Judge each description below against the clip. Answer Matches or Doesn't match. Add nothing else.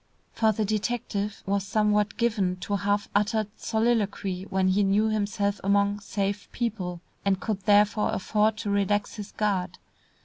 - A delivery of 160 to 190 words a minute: Doesn't match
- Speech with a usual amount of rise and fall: Doesn't match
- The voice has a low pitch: Doesn't match